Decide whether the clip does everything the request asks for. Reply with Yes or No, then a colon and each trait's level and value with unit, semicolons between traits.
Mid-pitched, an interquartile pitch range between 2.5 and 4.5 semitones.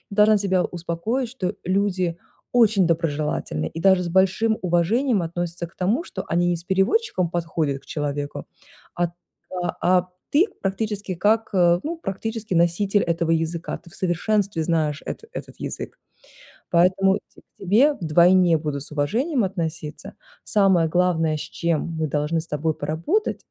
Yes: medium, 175 Hz; average, 3.4 semitones